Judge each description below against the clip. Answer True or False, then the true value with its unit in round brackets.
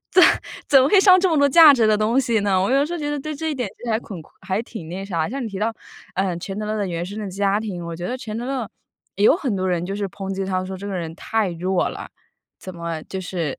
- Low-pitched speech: False (205 Hz)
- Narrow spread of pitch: False (5.1 semitones)